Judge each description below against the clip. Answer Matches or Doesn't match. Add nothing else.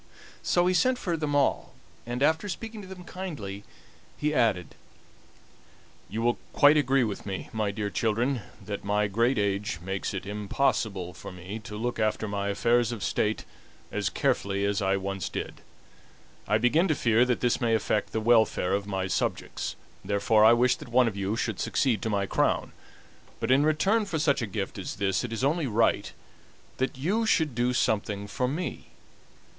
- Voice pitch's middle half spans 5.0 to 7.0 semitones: Matches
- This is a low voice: Matches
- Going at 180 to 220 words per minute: Matches